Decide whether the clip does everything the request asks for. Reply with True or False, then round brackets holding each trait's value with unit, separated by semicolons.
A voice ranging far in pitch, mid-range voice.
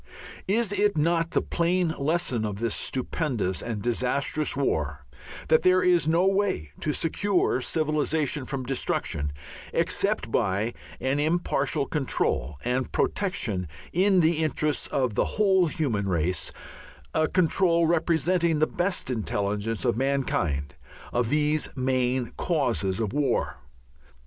True (6.6 semitones; 145 Hz)